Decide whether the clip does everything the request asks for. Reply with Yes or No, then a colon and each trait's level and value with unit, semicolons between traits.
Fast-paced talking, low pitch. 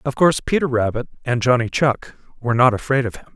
Yes: fast, 215 wpm; low, 125 Hz